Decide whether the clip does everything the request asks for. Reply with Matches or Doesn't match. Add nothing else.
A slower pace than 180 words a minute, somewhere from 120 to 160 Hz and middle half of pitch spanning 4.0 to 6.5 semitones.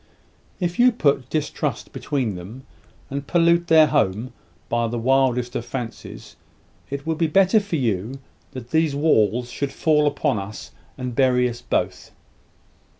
Matches